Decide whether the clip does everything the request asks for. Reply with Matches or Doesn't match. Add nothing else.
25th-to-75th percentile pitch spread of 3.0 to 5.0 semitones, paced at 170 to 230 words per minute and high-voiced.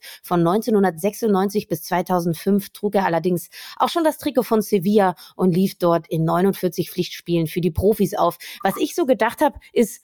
Matches